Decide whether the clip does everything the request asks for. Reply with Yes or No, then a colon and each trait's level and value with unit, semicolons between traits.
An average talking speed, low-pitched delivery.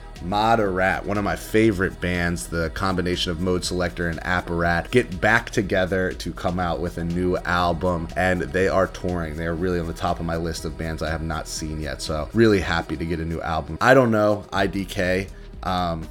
No: fast, 210 wpm; very low, 90 Hz